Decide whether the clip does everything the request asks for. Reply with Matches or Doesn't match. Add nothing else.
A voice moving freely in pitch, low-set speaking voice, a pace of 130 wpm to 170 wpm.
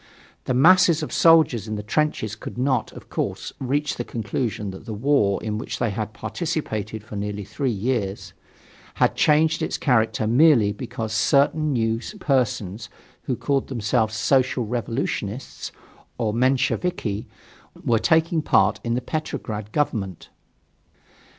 Doesn't match